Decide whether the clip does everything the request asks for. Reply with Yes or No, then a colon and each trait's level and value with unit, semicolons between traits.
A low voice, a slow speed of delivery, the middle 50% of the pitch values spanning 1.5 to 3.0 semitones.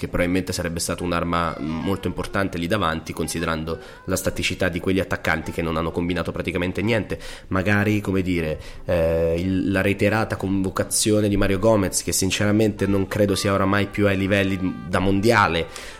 No: very low, 95 Hz; average, 160 wpm; narrow, 2.5 semitones